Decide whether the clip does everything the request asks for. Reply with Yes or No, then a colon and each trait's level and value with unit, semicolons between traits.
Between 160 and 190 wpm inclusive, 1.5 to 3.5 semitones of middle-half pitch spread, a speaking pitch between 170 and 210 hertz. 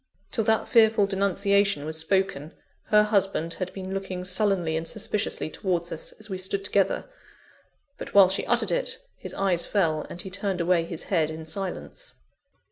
Yes: average, 170 wpm; average, 2.8 semitones; high, 190 Hz